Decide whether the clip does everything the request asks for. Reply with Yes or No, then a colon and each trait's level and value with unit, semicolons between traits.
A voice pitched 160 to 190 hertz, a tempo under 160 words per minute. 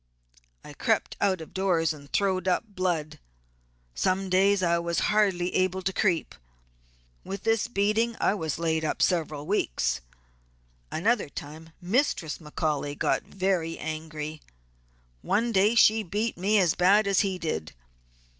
Yes: medium, 185 Hz; average, 140 wpm